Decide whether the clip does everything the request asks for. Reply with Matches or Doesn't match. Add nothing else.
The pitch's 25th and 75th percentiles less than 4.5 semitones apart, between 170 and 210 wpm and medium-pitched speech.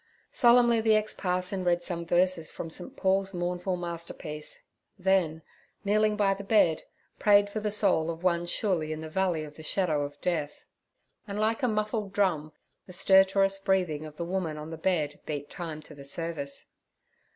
Matches